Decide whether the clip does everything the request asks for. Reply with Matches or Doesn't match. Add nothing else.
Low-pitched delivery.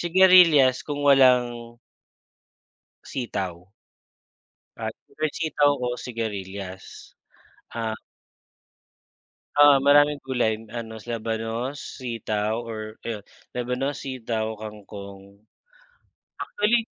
Matches